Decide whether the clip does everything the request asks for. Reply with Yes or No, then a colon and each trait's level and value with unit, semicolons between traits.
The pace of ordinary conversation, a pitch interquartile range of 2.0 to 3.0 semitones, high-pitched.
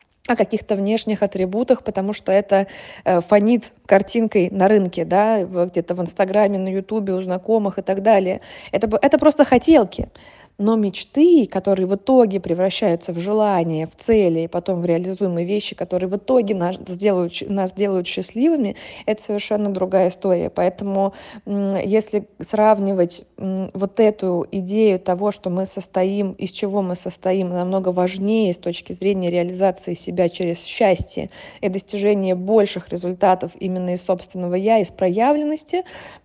Yes: average, 145 wpm; narrow, 2.4 semitones; high, 195 Hz